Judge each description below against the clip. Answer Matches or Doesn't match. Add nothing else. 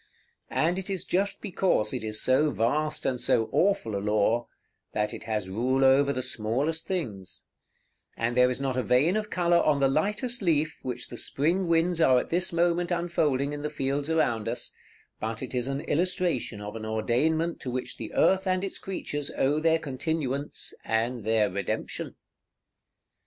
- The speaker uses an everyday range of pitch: Doesn't match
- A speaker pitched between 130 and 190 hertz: Matches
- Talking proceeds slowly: Doesn't match